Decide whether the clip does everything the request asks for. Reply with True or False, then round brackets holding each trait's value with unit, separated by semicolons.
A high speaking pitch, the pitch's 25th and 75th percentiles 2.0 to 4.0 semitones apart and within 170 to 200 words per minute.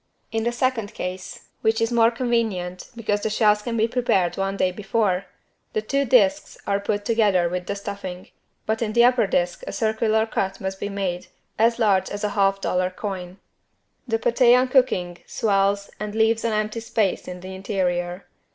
True (205 Hz; 3.2 semitones; 185 wpm)